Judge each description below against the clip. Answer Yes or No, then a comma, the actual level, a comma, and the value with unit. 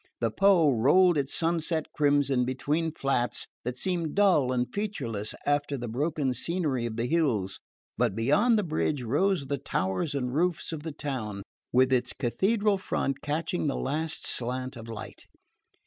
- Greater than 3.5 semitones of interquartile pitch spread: Yes, average, 5.0 semitones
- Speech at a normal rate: Yes, average, 160 wpm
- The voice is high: No, medium, 145 Hz